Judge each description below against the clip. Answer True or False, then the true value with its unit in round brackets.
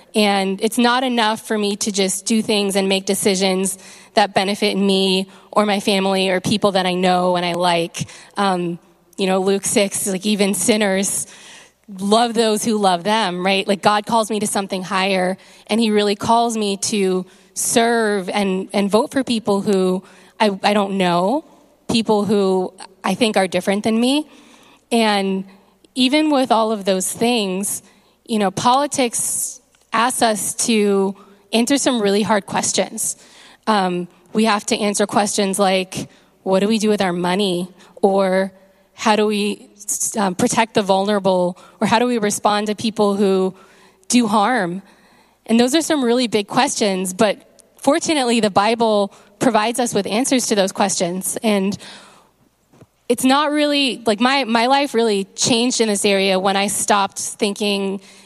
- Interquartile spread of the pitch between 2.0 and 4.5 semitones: True (2.8 semitones)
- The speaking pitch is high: True (205 Hz)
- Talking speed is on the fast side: False (165 wpm)